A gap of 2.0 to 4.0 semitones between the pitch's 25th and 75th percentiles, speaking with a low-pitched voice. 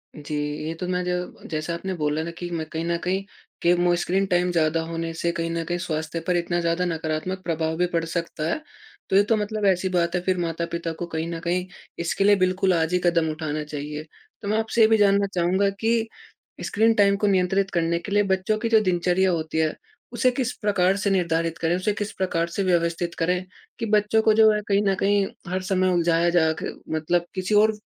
No: average, 2.8 semitones; medium, 180 Hz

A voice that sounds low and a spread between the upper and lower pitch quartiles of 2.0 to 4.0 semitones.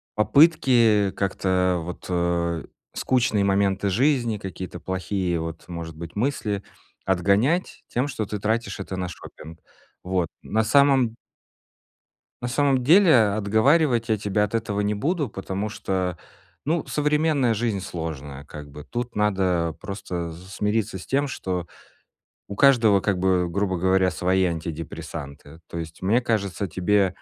No: low, 100 Hz; average, 4.5 semitones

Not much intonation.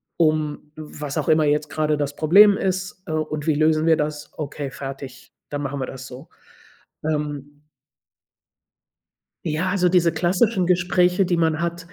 No: average, 3.2 semitones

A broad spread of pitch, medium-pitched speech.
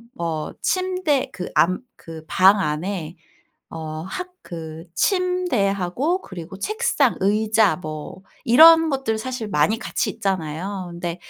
No: wide, 8.0 semitones; high, 195 Hz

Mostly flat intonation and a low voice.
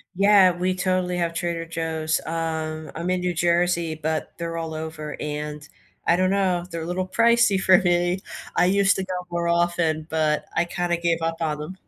No: narrow, 2.2 semitones; medium, 170 Hz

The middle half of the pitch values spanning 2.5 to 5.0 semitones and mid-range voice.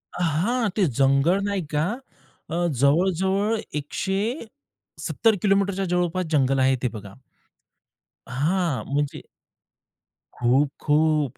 No: wide, 5.5 semitones; medium, 170 Hz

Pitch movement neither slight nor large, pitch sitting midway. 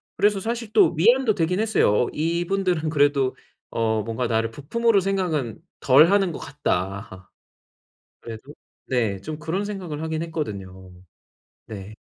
No: wide, 9.0 semitones; medium, 155 Hz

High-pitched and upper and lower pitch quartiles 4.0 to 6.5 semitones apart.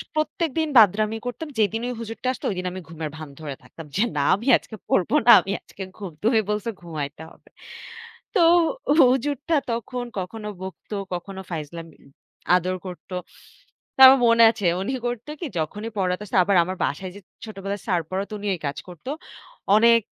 Yes: high, 200 Hz; average, 4.3 semitones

